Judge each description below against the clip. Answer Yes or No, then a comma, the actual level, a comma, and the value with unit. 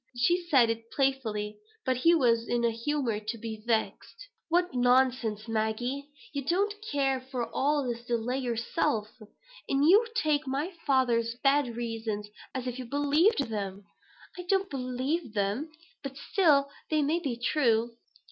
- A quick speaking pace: No, average, 155 wpm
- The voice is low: No, very high, 255 Hz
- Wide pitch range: No, average, 3.9 semitones